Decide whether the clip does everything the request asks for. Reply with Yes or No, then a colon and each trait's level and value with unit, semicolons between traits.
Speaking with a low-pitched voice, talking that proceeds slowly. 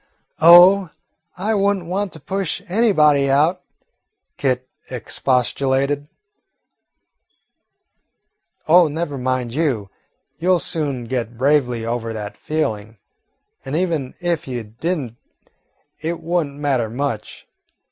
No: medium, 145 Hz; slow, 110 wpm